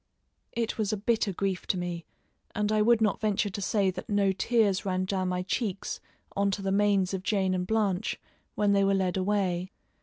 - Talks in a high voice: Yes, high, 195 Hz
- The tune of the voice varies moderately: No, narrow, 2.0 semitones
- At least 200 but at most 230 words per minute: Yes, fast, 205 wpm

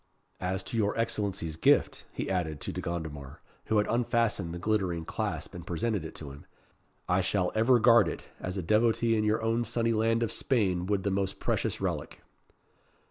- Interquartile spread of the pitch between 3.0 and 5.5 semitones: Yes, average, 4.4 semitones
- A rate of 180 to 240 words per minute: Yes, average, 190 wpm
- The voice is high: No, low, 100 Hz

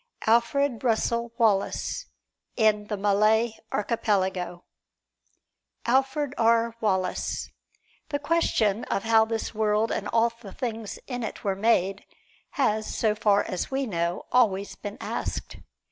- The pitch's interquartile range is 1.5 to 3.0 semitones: Yes, narrow, 2.5 semitones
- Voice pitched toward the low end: No, high, 220 Hz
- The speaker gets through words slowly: Yes, slow, 125 wpm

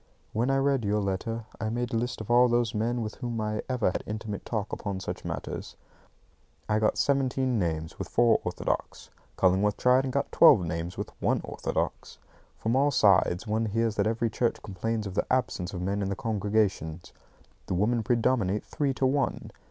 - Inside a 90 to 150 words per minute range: No, average, 190 wpm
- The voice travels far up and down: No, average, 3.4 semitones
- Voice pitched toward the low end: Yes, low, 110 Hz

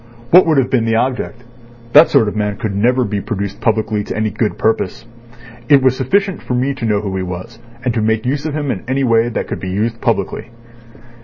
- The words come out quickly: Yes, fast, 230 wpm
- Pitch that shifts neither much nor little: Yes, average, 3.7 semitones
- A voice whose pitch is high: No, low, 115 Hz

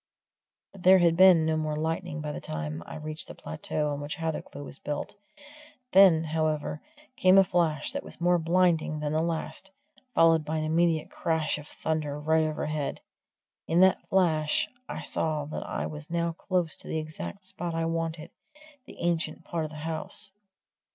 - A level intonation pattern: Yes, narrow, 1.9 semitones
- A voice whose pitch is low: No, medium, 160 Hz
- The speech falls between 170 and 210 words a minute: Yes, average, 180 wpm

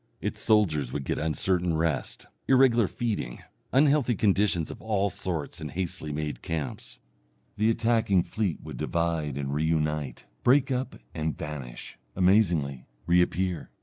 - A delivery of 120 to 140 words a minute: Yes, slow, 135 wpm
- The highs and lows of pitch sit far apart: Yes, wide, 6.0 semitones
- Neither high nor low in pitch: No, very low, 85 Hz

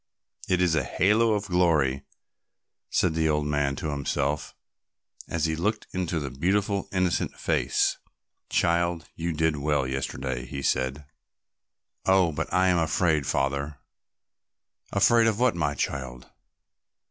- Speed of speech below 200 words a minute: Yes, slow, 135 wpm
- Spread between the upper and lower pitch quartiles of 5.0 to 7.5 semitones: No, average, 4.5 semitones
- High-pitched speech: No, very low, 80 Hz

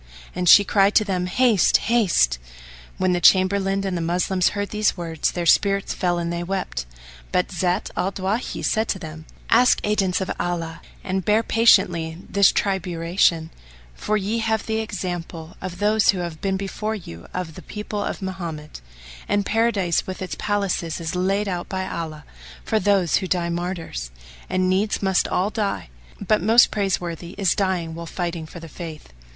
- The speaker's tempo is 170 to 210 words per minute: Yes, average, 175 wpm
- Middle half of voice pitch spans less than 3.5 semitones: Yes, average, 3.0 semitones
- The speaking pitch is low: No, medium, 185 Hz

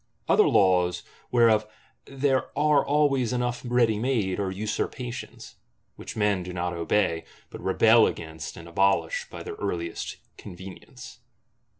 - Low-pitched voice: Yes, low, 105 Hz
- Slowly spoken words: Yes, slow, 125 wpm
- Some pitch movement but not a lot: No, wide, 5.8 semitones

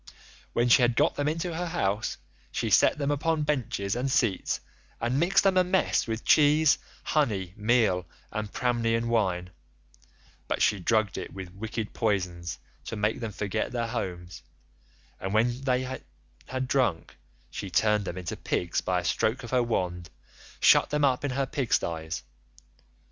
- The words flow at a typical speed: Yes, average, 165 wpm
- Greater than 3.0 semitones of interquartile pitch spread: Yes, wide, 5.6 semitones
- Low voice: Yes, low, 115 Hz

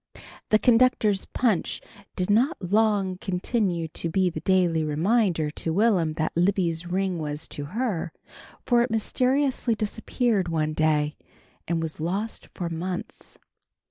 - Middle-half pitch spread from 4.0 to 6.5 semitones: Yes, average, 5.1 semitones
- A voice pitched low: No, medium, 185 Hz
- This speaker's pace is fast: No, slow, 135 wpm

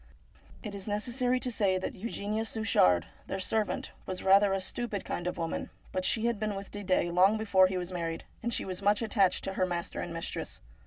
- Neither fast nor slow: No, fast, 210 wpm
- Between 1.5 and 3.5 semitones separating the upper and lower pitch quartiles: Yes, average, 2.8 semitones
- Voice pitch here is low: No, high, 195 Hz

